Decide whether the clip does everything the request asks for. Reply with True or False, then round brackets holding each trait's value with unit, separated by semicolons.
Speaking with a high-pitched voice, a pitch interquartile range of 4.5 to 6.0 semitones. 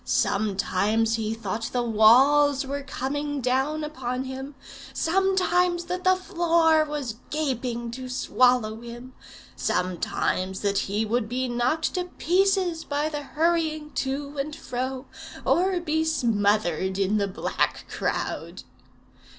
True (265 Hz; 5.6 semitones)